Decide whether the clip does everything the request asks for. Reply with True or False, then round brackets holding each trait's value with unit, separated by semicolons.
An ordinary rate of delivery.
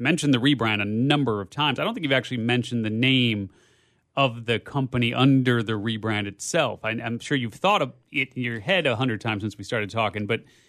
False (225 wpm)